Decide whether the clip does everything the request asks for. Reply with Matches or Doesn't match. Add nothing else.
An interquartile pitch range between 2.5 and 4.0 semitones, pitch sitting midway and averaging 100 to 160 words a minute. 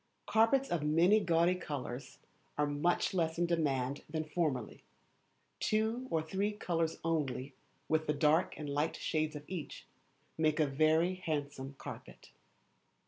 Matches